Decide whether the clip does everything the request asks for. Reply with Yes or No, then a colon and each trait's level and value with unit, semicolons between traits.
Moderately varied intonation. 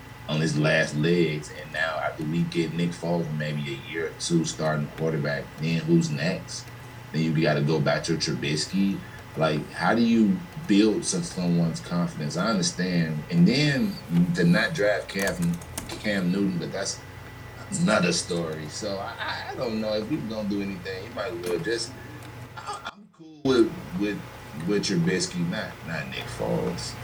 No: wide, 6.6 semitones